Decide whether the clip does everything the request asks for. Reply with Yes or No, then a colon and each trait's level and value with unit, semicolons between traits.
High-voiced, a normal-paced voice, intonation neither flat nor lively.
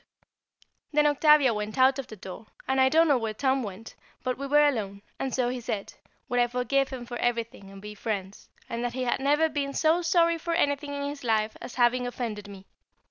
No: very high, 255 Hz; fast, 230 wpm; average, 4.3 semitones